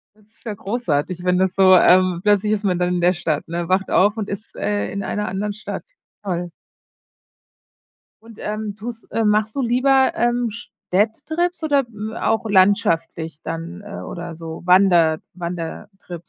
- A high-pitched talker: Yes, high, 195 Hz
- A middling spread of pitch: Yes, average, 3.6 semitones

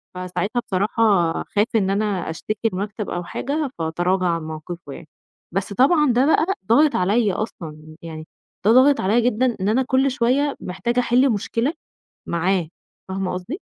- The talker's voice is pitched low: No, high, 205 Hz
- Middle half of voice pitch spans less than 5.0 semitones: No, wide, 5.5 semitones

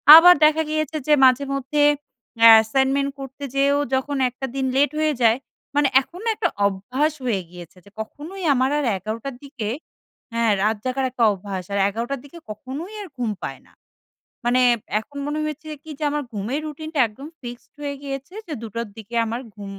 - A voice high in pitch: Yes, very high, 265 Hz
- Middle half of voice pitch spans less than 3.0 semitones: No, average, 4.3 semitones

